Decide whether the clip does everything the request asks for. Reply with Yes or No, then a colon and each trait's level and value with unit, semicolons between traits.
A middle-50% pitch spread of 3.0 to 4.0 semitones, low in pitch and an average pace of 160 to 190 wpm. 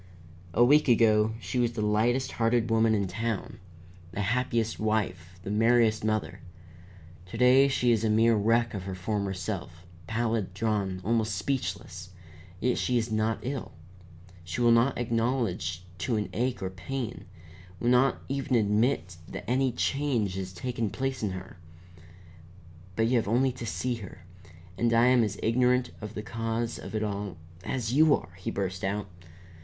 Yes: average, 3.3 semitones; low, 115 Hz; average, 170 wpm